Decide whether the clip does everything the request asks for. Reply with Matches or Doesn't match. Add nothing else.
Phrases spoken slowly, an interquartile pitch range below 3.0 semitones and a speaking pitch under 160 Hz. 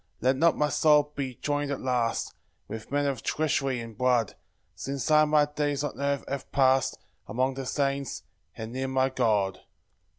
Doesn't match